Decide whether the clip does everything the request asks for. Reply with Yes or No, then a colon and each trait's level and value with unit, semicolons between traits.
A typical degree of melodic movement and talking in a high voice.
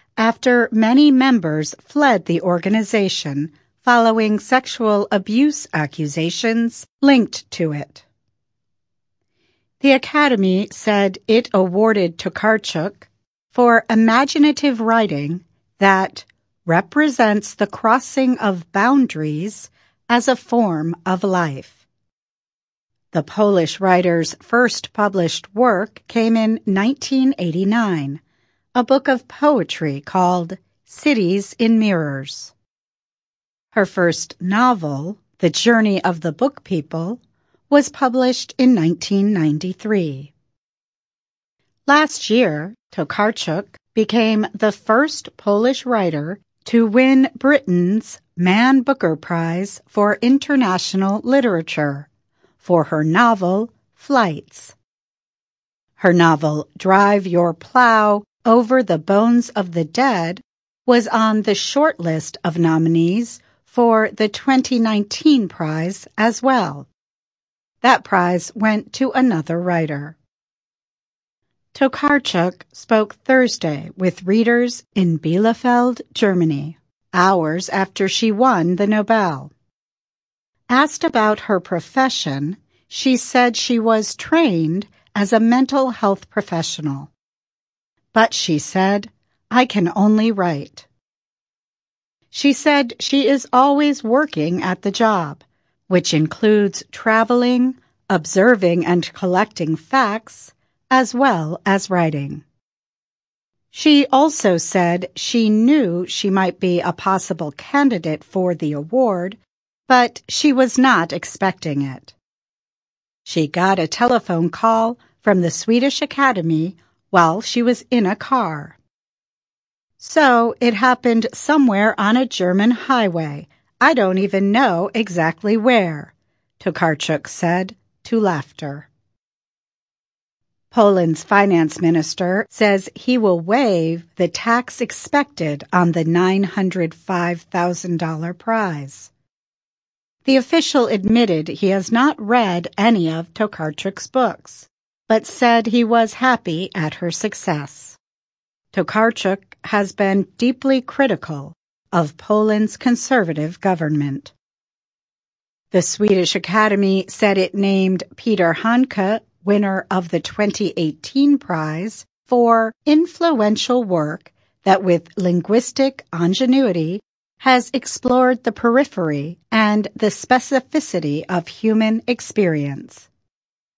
No: wide, 5.8 semitones; high, 200 Hz